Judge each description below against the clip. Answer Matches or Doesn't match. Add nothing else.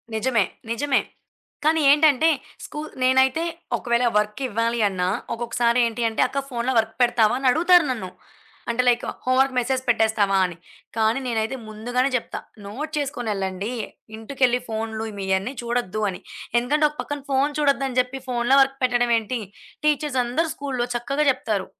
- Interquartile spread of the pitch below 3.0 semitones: Doesn't match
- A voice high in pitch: Matches